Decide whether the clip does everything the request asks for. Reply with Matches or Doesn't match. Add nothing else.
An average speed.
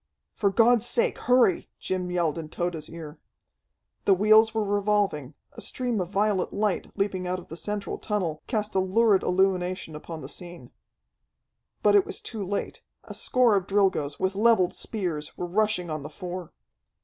Matches